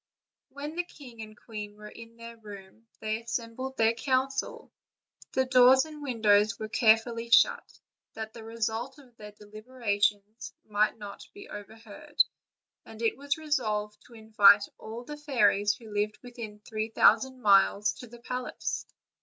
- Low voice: No, high, 225 Hz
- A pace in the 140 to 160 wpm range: Yes, average, 150 wpm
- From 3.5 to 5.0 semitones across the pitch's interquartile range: No, average, 3.1 semitones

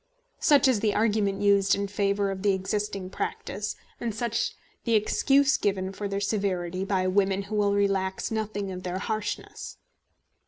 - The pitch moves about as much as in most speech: No, narrow, 1.6 semitones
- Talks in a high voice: Yes, high, 200 Hz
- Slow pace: No, average, 160 wpm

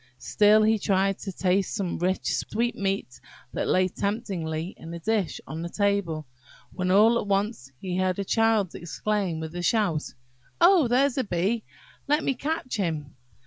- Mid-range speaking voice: No, high, 195 Hz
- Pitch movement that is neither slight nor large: Yes, average, 4.0 semitones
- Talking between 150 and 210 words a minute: Yes, average, 165 wpm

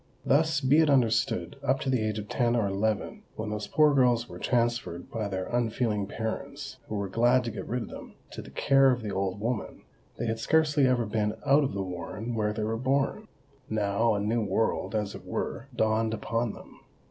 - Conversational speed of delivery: No, fast, 210 wpm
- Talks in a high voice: No, low, 115 Hz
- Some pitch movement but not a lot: Yes, average, 3.5 semitones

